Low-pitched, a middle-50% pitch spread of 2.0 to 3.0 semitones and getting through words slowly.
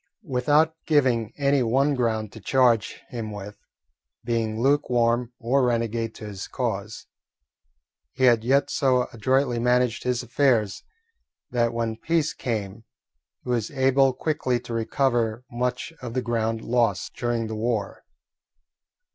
Yes: low, 120 Hz; narrow, 2.5 semitones; slow, 130 wpm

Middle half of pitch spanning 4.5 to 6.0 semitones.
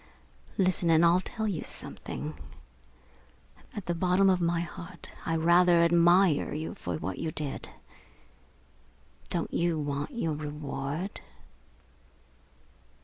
No: average, 3.0 semitones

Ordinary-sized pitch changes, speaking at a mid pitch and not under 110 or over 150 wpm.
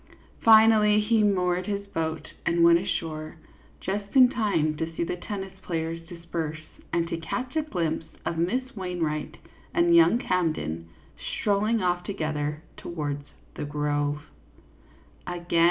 Yes: average, 4.8 semitones; medium, 175 Hz; average, 140 wpm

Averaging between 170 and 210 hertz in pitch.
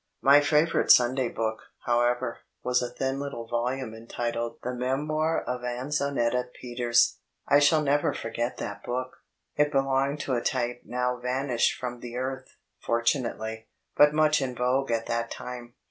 No: low, 125 Hz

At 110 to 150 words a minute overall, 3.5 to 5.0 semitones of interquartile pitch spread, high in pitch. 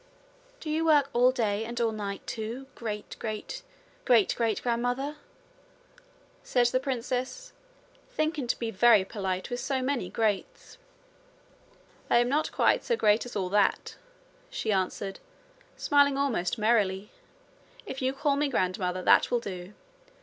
Yes: average, 140 wpm; average, 4.6 semitones; high, 235 Hz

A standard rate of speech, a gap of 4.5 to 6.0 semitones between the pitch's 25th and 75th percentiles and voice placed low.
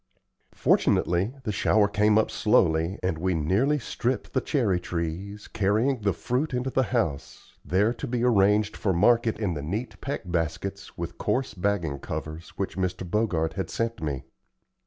Yes: average, 160 wpm; average, 5.0 semitones; low, 100 Hz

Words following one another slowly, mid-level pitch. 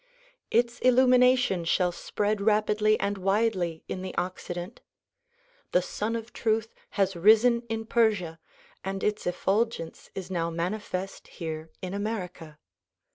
No: slow, 125 wpm; high, 200 Hz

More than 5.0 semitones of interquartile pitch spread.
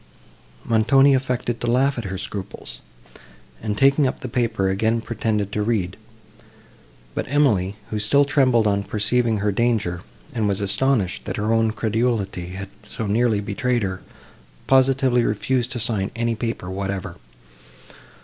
No: average, 3.6 semitones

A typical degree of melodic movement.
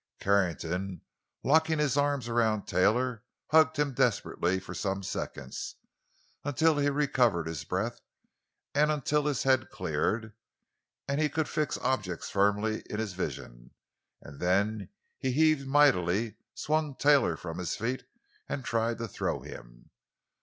No: wide, 7.2 semitones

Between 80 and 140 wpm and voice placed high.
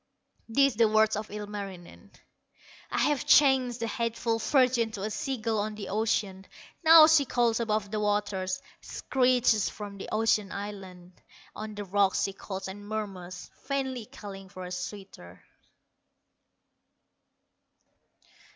Yes: slow, 135 wpm; high, 210 Hz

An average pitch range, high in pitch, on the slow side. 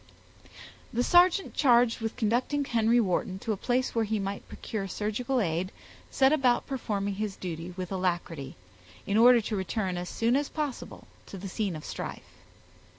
No: average, 4.5 semitones; high, 215 Hz; average, 165 wpm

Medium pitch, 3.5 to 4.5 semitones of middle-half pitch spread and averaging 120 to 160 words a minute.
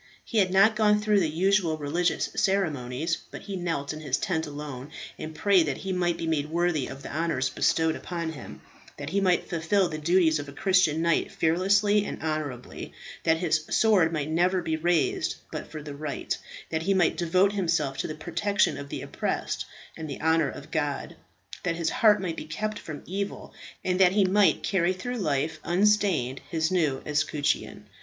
No: medium, 165 Hz; average, 3.8 semitones; average, 190 wpm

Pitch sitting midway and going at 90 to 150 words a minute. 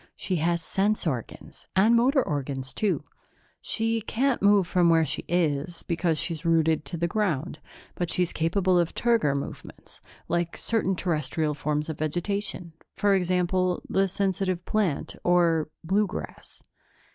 Yes: medium, 175 Hz; average, 145 wpm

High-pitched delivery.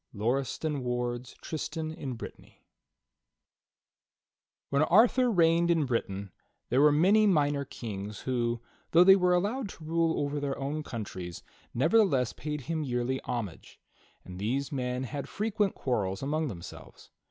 No: medium, 140 Hz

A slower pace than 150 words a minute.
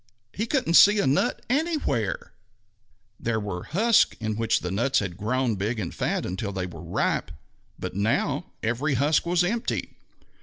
No: average, 165 wpm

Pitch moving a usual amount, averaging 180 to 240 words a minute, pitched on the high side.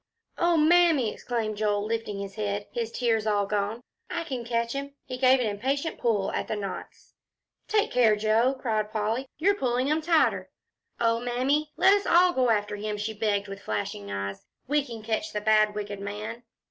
Yes: average, 4.4 semitones; average, 190 wpm; high, 230 Hz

